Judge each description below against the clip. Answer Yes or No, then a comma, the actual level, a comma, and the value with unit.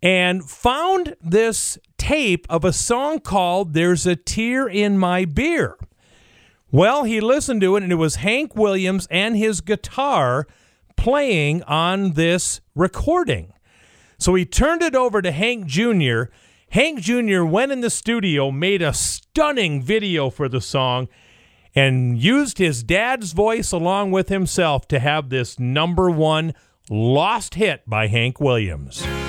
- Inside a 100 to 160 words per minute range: Yes, average, 145 wpm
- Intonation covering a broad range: Yes, wide, 7.2 semitones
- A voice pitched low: No, medium, 180 Hz